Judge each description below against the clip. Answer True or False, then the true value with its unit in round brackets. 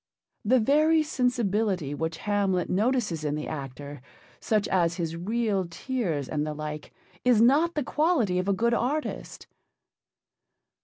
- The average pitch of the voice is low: False (200 Hz)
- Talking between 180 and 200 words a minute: False (140 wpm)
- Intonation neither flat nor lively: False (7.4 semitones)